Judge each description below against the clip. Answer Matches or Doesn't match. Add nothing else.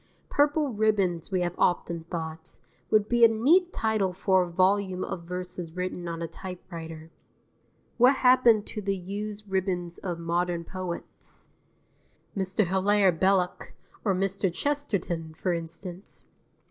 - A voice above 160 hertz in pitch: Matches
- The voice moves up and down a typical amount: Matches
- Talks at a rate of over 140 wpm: Doesn't match